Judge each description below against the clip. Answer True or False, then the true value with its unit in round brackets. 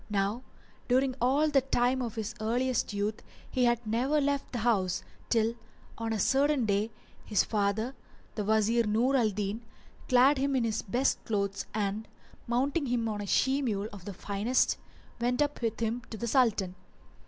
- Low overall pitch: False (230 Hz)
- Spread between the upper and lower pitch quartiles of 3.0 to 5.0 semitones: True (3.5 semitones)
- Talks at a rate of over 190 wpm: False (175 wpm)